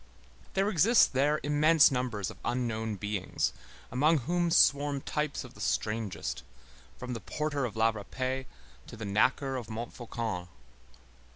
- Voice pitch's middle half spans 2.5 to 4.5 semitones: No, average, 4.9 semitones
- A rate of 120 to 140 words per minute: Yes, slow, 135 wpm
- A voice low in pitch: Yes, low, 125 Hz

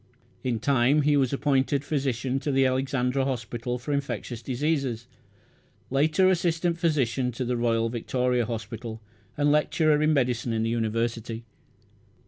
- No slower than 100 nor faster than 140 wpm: Yes, slow, 135 wpm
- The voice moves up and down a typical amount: Yes, average, 3.5 semitones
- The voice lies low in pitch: Yes, low, 130 Hz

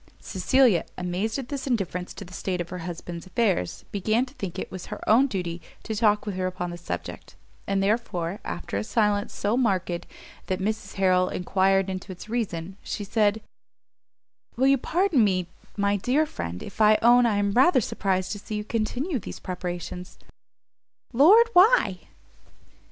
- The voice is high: Yes, high, 200 Hz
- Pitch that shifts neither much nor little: Yes, average, 4.3 semitones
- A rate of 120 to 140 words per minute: No, average, 170 wpm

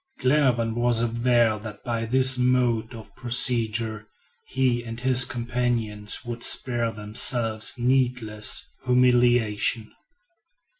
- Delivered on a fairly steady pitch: Yes, narrow, 1.9 semitones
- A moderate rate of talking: No, slow, 100 wpm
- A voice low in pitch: Yes, low, 120 Hz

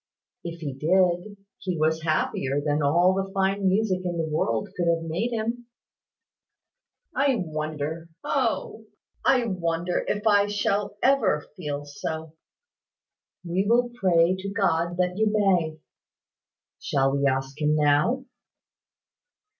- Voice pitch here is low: No, medium, 175 Hz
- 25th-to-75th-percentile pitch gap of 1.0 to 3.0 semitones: No, average, 4.6 semitones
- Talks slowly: Yes, slow, 130 wpm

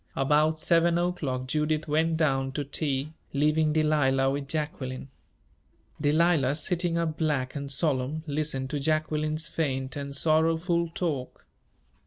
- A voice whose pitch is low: No, medium, 150 Hz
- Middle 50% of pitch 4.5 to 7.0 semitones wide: No, narrow, 2.5 semitones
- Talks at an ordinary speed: No, slow, 125 wpm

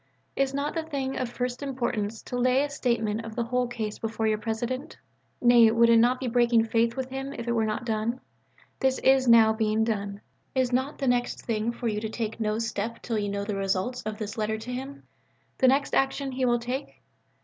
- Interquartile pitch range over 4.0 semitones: No, average, 2.8 semitones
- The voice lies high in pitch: Yes, high, 235 Hz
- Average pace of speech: No, fast, 220 wpm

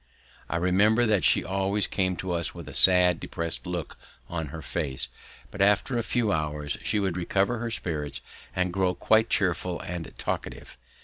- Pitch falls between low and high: No, very low, 90 Hz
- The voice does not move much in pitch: No, average, 3.3 semitones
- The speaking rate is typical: Yes, average, 175 wpm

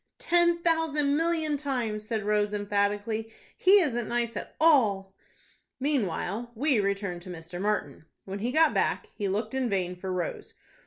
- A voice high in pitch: Yes, high, 220 Hz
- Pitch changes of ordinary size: No, wide, 6.5 semitones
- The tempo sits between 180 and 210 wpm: No, average, 155 wpm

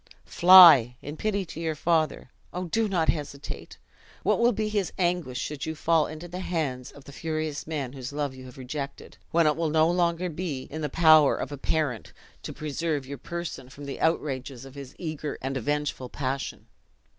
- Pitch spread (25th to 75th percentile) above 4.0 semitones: No, average, 3.4 semitones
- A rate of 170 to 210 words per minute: Yes, average, 190 wpm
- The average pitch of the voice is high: No, medium, 155 Hz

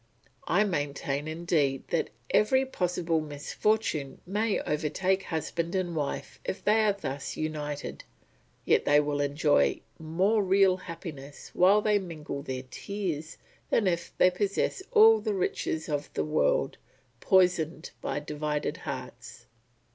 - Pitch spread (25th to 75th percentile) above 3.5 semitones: Yes, average, 4.7 semitones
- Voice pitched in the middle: Yes, medium, 165 Hz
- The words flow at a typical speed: No, slow, 130 wpm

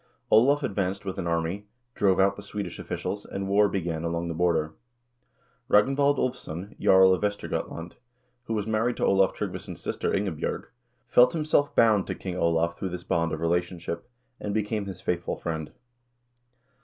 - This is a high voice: No, very low, 95 Hz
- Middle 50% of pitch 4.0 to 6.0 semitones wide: No, average, 3.5 semitones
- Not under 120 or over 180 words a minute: Yes, average, 165 wpm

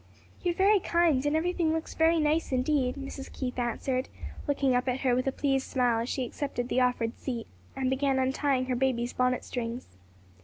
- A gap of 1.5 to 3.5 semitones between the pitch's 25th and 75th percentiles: Yes, average, 2.7 semitones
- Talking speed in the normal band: Yes, average, 195 wpm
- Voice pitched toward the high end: Yes, very high, 265 Hz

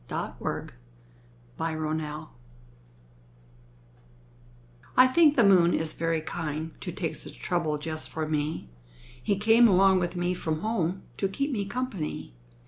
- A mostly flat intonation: No, average, 4.2 semitones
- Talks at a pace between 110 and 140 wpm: Yes, slow, 135 wpm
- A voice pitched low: No, medium, 175 Hz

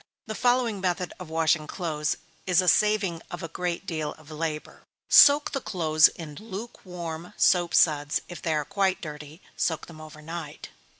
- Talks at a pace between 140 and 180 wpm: Yes, average, 170 wpm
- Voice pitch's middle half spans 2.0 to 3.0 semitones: No, average, 3.4 semitones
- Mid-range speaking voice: Yes, medium, 170 Hz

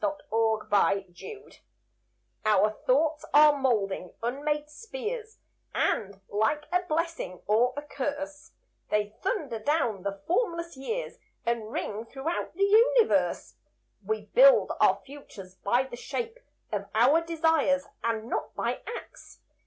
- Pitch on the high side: Yes, very high, 285 Hz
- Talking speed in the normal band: No, slow, 130 wpm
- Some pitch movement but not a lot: No, wide, 7.4 semitones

